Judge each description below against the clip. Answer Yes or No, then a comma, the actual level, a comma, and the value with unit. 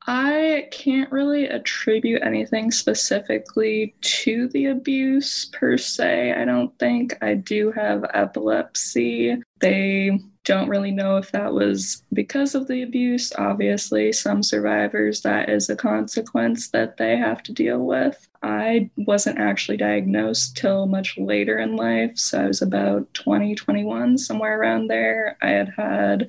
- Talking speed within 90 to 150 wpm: Yes, average, 145 wpm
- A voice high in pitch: No, low, 130 Hz